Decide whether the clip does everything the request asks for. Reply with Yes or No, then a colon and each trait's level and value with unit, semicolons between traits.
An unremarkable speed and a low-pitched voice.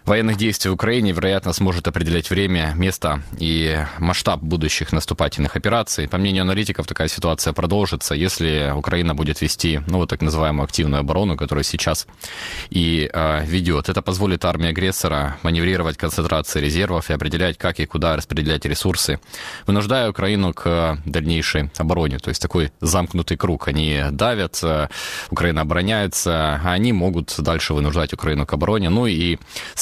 Yes: average, 145 wpm; very low, 85 Hz